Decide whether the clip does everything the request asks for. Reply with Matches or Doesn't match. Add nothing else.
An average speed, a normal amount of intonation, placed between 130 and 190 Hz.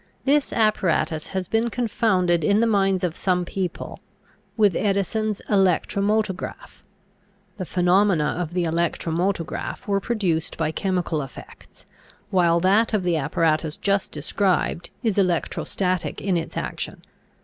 Doesn't match